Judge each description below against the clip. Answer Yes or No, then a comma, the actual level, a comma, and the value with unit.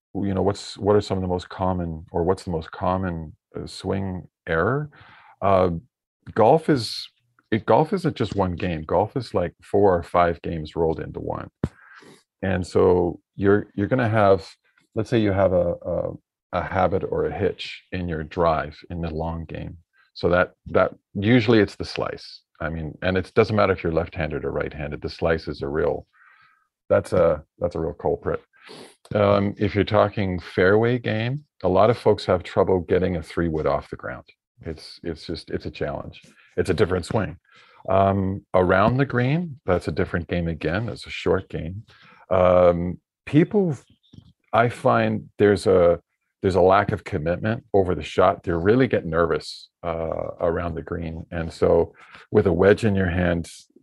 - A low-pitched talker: Yes, very low, 95 Hz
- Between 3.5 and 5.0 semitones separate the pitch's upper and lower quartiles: Yes, average, 3.8 semitones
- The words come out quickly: No, average, 180 wpm